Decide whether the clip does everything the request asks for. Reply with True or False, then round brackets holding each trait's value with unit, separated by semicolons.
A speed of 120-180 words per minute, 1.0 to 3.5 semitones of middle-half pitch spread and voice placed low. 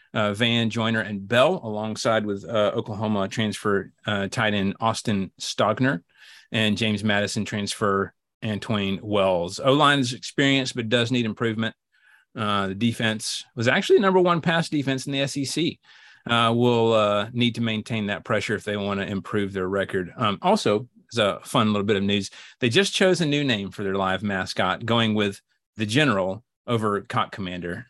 True (170 wpm; 3.0 semitones; 110 Hz)